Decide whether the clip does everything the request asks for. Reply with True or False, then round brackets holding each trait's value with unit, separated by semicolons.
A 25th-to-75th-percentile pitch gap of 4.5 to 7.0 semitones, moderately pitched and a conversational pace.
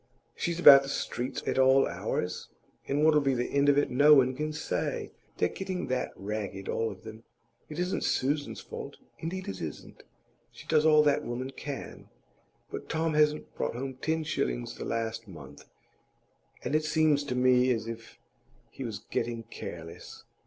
False (4.9 semitones; 130 Hz; 175 wpm)